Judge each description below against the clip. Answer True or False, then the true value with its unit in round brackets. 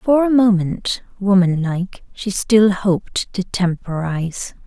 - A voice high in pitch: True (195 Hz)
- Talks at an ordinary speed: False (105 wpm)